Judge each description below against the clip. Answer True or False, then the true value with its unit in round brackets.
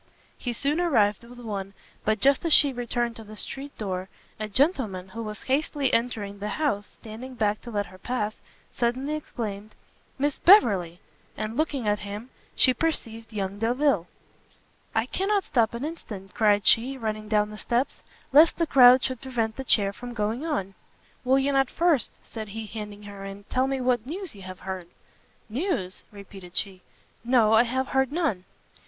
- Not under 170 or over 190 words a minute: True (175 wpm)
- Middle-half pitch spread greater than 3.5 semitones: True (4.5 semitones)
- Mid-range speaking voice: False (230 Hz)